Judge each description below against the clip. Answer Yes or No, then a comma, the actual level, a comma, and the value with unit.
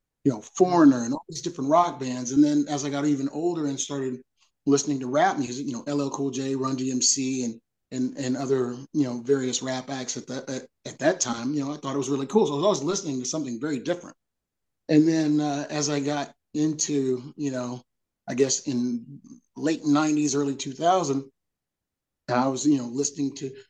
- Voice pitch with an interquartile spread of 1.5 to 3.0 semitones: Yes, narrow, 2.4 semitones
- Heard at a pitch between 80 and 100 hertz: No, medium, 140 Hz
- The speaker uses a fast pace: Yes, fast, 210 wpm